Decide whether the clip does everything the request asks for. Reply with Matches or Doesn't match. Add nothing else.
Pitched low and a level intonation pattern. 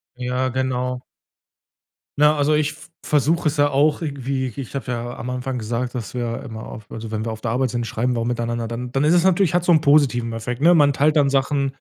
Doesn't match